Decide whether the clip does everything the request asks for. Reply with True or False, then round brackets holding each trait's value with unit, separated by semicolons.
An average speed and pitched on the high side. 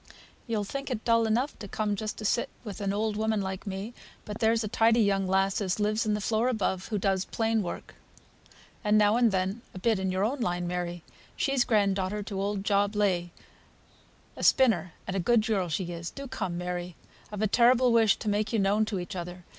False (220 wpm; 205 Hz)